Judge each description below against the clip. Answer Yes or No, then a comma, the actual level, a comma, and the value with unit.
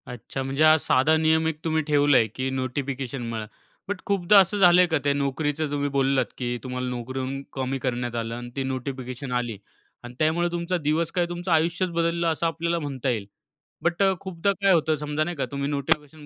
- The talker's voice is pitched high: No, medium, 145 Hz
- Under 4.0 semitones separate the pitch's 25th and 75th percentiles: No, average, 4.4 semitones